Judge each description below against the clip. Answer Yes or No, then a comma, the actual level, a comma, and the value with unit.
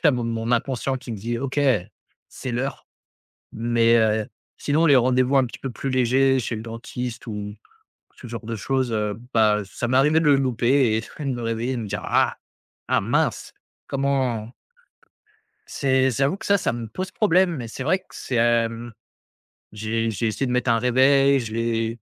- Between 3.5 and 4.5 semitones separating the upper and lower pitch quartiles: No, average, 2.8 semitones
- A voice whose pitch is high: No, low, 120 Hz